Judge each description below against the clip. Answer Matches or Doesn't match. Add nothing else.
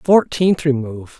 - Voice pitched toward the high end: Doesn't match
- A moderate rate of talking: Matches